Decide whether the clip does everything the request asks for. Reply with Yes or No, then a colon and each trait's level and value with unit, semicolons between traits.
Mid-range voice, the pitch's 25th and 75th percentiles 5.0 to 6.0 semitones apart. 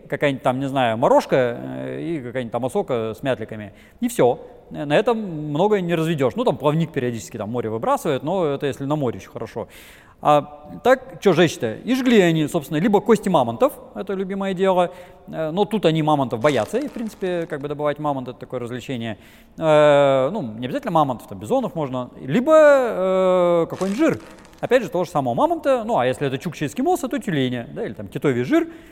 No: medium, 160 Hz; wide, 7.3 semitones